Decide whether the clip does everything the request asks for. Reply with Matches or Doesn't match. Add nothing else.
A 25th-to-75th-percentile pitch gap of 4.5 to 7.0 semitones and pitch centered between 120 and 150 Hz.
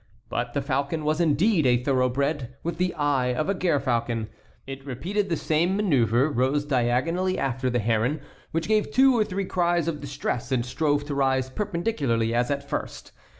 Matches